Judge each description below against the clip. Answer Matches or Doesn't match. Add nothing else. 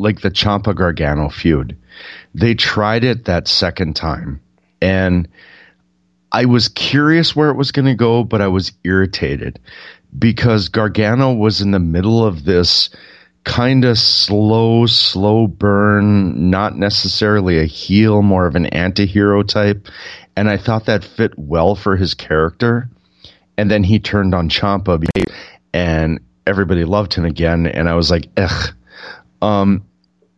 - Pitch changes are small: Doesn't match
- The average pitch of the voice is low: Matches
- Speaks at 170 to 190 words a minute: Doesn't match